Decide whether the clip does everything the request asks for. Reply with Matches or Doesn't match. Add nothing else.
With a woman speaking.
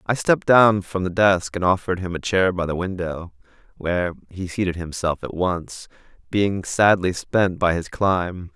Doesn't match